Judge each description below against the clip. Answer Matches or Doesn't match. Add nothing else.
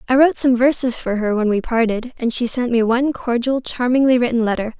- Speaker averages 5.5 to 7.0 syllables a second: Matches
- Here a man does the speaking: Doesn't match